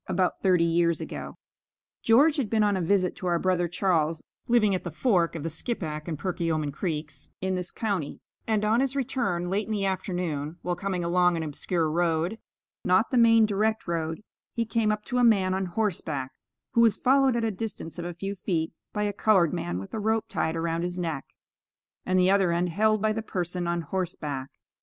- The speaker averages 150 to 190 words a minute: No, fast, 205 wpm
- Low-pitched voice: No, medium, 185 Hz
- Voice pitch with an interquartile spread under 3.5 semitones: No, average, 4.2 semitones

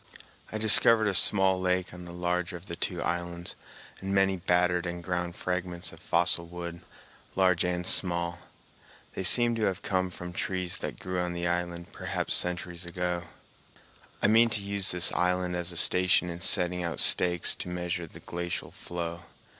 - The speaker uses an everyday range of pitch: No, narrow, 1.1 semitones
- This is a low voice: Yes, very low, 90 Hz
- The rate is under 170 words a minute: No, average, 175 wpm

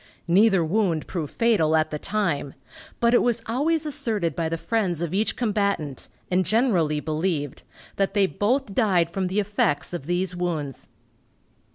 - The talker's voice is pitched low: No, medium, 185 Hz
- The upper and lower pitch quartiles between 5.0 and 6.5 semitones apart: Yes, average, 5.3 semitones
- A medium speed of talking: Yes, average, 160 wpm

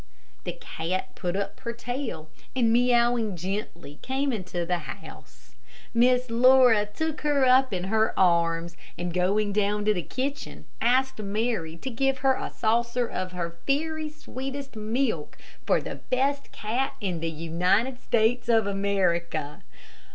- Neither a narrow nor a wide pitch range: No, wide, 5.9 semitones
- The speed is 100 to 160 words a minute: Yes, average, 145 wpm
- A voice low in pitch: No, high, 220 Hz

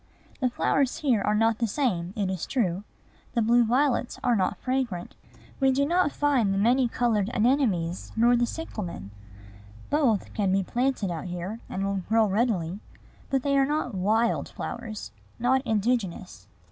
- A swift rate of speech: No, average, 160 wpm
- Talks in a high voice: Yes, high, 225 Hz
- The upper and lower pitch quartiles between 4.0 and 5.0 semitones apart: Yes, average, 4.7 semitones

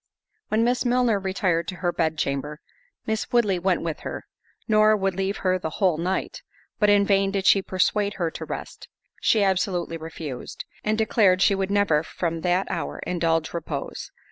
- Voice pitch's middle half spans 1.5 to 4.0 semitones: Yes, average, 3.5 semitones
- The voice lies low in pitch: No, high, 190 Hz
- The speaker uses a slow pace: No, average, 170 wpm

